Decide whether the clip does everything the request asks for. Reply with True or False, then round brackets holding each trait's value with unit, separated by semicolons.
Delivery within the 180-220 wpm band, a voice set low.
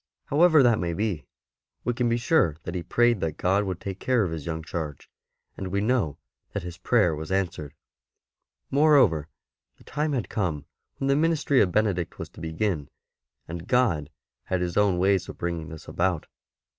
True (185 wpm; 95 Hz)